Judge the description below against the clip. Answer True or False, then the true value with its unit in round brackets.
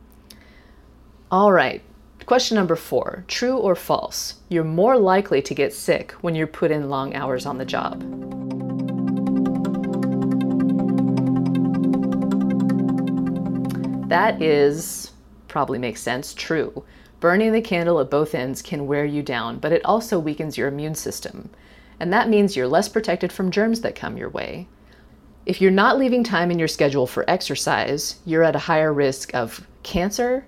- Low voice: False (145 Hz)